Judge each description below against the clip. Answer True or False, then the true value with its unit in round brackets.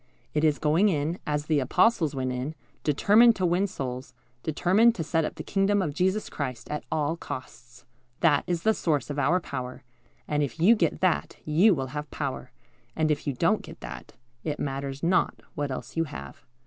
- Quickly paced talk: False (195 wpm)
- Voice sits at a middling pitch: True (150 Hz)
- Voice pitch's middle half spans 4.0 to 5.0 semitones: True (4.6 semitones)